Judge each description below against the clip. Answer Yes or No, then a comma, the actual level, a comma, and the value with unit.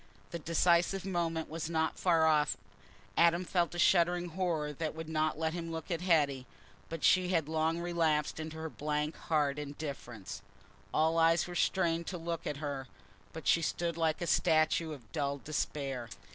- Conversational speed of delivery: Yes, average, 175 wpm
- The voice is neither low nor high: Yes, medium, 160 Hz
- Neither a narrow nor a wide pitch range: No, narrow, 2.1 semitones